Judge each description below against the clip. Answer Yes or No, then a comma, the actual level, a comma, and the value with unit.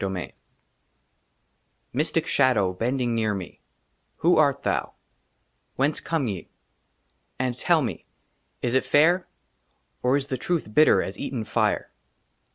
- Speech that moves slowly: Yes, slow, 130 wpm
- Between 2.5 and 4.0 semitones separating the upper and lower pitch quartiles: No, average, 5.0 semitones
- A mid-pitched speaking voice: No, low, 130 Hz